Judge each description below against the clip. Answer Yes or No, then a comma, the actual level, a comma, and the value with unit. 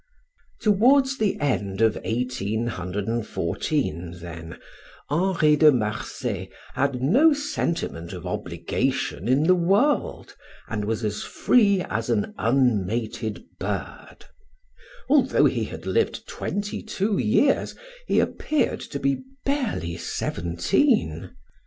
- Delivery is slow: Yes, slow, 105 wpm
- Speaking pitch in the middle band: No, low, 125 Hz